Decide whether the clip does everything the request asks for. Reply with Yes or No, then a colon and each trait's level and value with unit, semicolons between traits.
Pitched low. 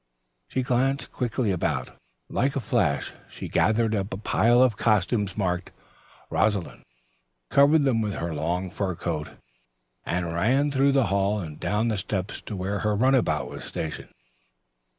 Yes: low, 105 Hz